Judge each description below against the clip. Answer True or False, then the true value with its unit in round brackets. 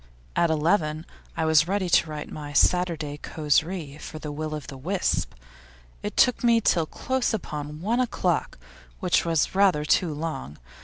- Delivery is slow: False (160 wpm)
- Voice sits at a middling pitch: True (160 Hz)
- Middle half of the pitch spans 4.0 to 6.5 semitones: False (3.6 semitones)